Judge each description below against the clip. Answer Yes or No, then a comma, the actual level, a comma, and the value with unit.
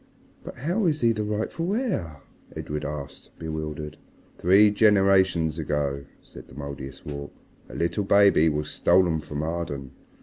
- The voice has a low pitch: Yes, very low, 80 Hz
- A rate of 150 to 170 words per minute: No, slow, 135 wpm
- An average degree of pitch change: No, wide, 5.7 semitones